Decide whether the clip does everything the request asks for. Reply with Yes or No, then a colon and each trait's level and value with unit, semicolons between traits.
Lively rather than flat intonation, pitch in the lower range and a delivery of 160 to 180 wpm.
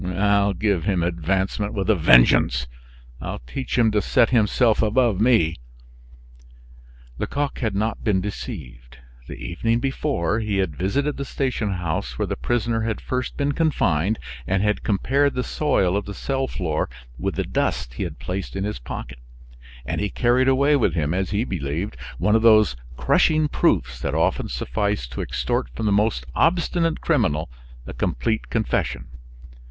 Yes: wide, 5.7 semitones; low, 105 Hz; average, 165 wpm